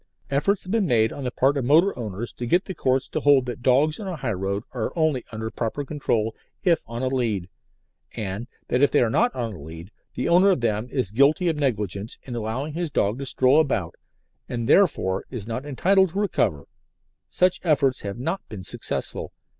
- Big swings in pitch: Yes, wide, 5.8 semitones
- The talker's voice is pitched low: Yes, low, 130 Hz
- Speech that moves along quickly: Yes, fast, 210 wpm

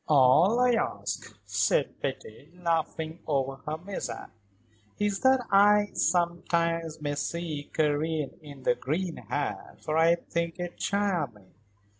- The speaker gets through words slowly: Yes, slow, 125 wpm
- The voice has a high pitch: No, medium, 160 Hz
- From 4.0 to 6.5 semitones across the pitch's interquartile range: No, average, 3.6 semitones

